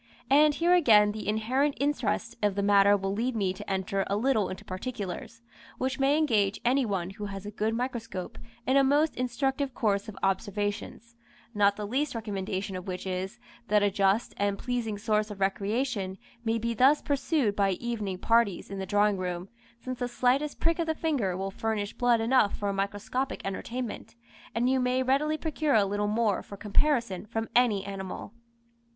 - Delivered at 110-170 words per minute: No, average, 185 wpm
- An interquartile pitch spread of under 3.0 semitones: No, average, 4.3 semitones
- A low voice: No, high, 215 Hz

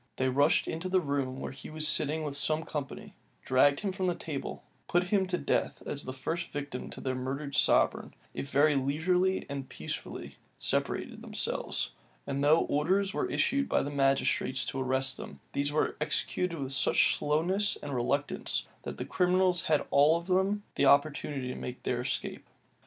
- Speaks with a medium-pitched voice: Yes, medium, 145 Hz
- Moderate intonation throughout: Yes, average, 4.5 semitones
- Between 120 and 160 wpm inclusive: No, average, 180 wpm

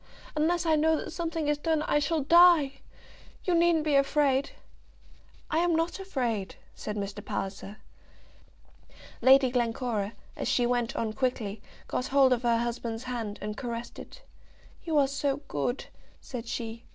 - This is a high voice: Yes, very high, 265 Hz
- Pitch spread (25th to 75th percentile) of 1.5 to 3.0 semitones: No, average, 5.1 semitones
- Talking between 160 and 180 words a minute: No, average, 150 wpm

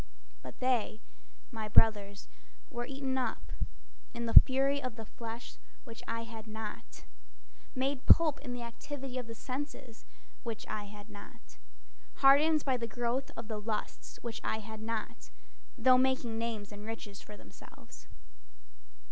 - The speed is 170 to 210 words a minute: No, average, 145 wpm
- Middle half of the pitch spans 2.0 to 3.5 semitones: Yes, average, 3.2 semitones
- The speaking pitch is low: No, high, 230 Hz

